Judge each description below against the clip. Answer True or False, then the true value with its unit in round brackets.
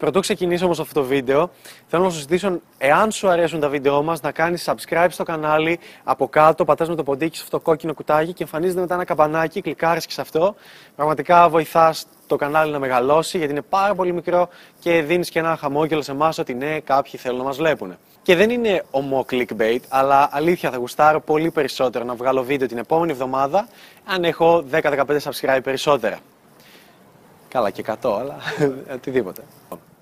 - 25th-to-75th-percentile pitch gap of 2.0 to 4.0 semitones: True (3.4 semitones)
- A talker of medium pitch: True (155 Hz)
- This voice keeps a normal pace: False (185 wpm)